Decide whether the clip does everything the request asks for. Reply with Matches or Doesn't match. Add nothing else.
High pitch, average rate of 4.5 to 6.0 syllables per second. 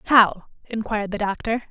Matches